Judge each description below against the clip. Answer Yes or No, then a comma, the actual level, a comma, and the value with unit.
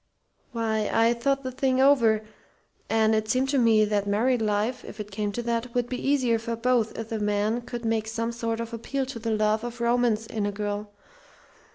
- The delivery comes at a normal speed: No, fast, 210 wpm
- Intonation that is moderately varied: No, narrow, 2.1 semitones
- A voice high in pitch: Yes, high, 230 Hz